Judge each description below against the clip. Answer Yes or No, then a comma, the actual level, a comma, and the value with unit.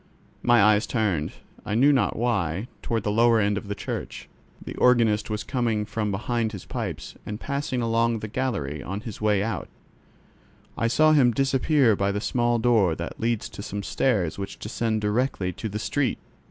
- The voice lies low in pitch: Yes, low, 110 Hz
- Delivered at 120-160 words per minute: No, average, 180 wpm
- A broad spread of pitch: No, average, 2.8 semitones